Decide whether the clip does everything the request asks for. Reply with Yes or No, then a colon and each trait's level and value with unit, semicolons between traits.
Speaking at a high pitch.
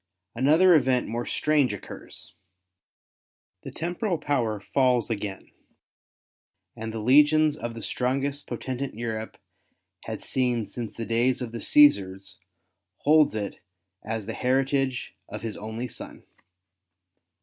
No: low, 125 Hz